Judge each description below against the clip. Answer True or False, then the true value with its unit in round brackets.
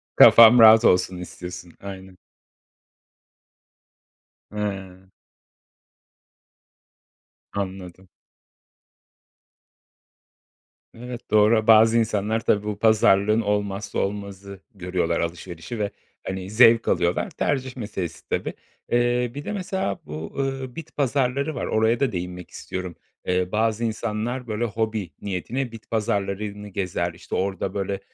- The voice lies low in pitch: True (105 Hz)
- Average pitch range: True (3.5 semitones)